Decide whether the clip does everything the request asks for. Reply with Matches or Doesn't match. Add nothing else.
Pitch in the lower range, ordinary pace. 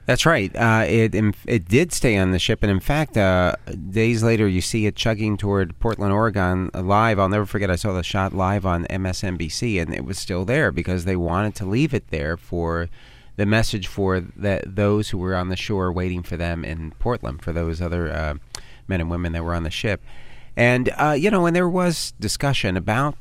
Doesn't match